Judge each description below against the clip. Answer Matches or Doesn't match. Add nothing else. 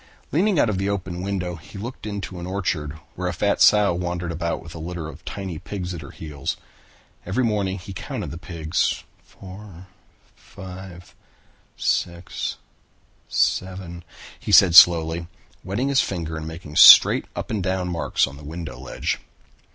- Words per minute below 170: Matches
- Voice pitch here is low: Matches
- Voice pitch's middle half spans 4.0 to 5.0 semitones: Doesn't match